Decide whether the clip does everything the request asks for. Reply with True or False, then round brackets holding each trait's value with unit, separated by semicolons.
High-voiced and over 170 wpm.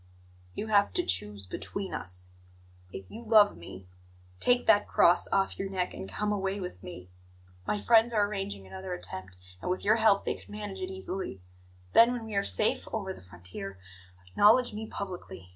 True (195 Hz; 180 wpm)